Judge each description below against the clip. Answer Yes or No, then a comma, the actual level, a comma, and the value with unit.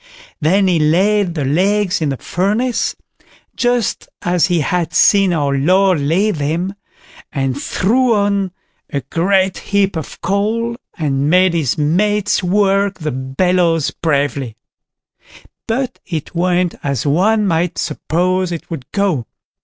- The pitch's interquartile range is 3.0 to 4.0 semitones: No, average, 4.6 semitones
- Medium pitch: Yes, medium, 180 Hz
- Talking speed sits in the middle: No, slow, 130 wpm